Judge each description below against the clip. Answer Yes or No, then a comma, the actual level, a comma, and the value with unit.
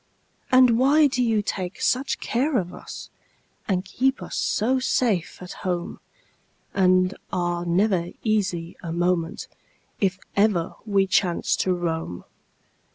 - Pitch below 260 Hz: Yes, high, 190 Hz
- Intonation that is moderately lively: Yes, average, 4.8 semitones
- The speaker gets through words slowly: Yes, slow, 130 wpm